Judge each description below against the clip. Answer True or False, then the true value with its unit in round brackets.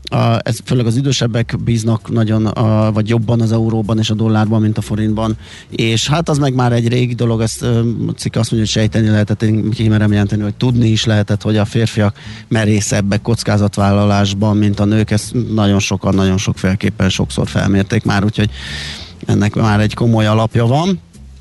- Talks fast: True (175 wpm)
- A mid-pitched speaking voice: False (110 Hz)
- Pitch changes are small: True (2.0 semitones)